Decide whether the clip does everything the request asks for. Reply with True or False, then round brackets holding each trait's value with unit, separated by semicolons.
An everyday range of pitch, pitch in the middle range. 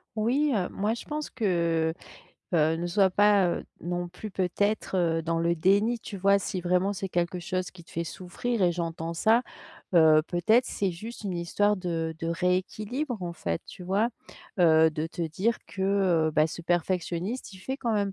True (3.5 semitones; 180 Hz)